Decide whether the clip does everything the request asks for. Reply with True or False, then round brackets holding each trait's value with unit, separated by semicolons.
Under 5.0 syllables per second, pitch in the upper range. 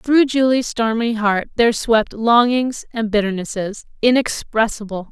True (4.4 syllables/s; 225 Hz)